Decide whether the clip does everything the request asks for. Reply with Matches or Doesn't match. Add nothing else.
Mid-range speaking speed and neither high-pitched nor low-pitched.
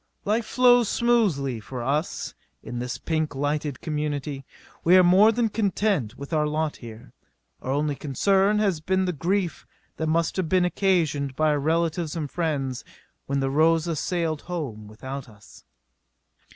Matches